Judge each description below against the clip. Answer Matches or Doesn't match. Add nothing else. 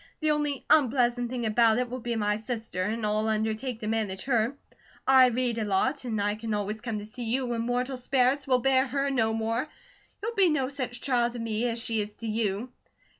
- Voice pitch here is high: Matches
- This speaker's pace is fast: Matches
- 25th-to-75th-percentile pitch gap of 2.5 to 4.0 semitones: Matches